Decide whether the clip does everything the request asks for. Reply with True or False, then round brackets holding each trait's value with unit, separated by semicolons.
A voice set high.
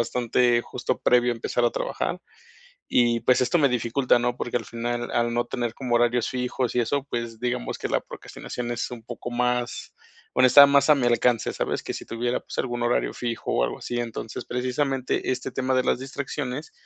False (120 Hz)